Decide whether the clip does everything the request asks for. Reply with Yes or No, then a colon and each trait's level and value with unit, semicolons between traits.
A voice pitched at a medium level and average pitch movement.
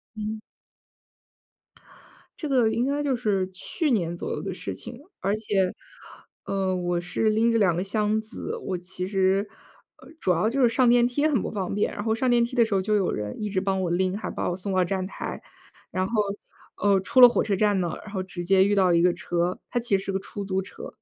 No: high, 200 Hz; average, 3.2 semitones